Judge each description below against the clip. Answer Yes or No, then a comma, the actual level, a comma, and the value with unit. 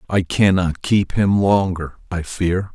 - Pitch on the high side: No, very low, 95 Hz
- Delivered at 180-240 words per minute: No, average, 155 wpm